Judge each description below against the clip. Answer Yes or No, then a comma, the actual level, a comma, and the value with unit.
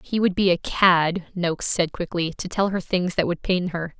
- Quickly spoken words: Yes, fast, 240 wpm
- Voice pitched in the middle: Yes, medium, 180 Hz